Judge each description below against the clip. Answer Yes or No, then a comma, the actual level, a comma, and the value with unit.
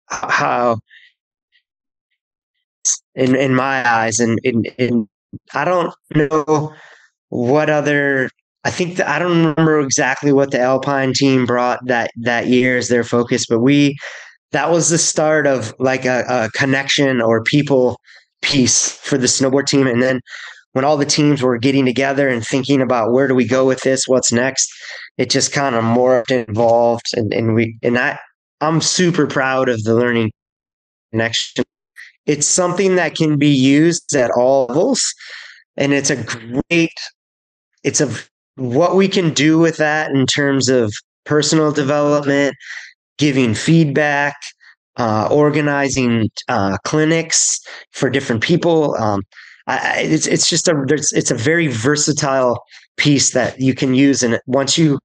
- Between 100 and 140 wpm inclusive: No, average, 155 wpm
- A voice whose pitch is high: No, low, 135 Hz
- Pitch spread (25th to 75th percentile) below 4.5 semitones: Yes, average, 3.5 semitones